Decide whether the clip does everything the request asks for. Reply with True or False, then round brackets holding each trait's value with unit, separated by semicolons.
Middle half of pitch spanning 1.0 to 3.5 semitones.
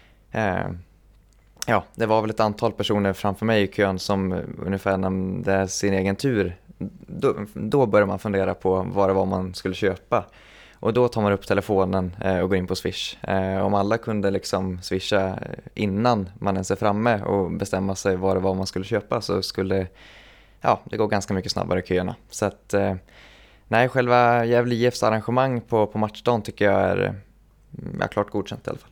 True (2.4 semitones)